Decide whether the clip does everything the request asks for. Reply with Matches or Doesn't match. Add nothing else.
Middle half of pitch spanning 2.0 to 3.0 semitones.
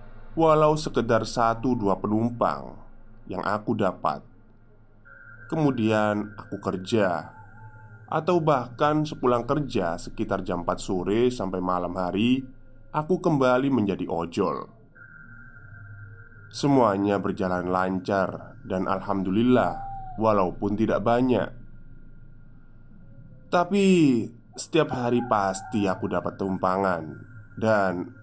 Doesn't match